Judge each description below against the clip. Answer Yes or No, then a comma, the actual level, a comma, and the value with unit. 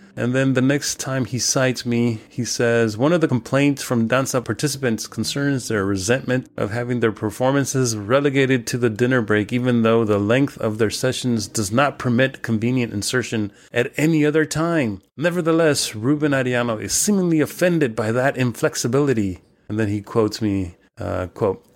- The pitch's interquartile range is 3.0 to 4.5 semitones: Yes, average, 3.5 semitones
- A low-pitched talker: Yes, low, 125 Hz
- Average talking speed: Yes, average, 170 wpm